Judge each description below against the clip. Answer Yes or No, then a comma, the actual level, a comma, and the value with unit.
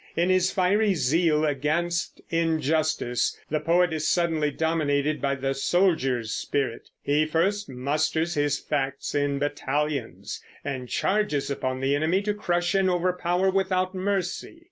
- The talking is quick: No, slow, 135 wpm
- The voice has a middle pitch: Yes, medium, 160 Hz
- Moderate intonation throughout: Yes, average, 4.0 semitones